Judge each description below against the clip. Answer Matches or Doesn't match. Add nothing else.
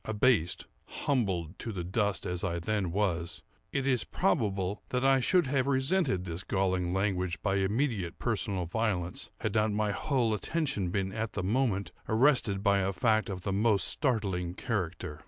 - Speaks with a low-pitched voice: Matches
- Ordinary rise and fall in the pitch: Matches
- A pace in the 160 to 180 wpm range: Matches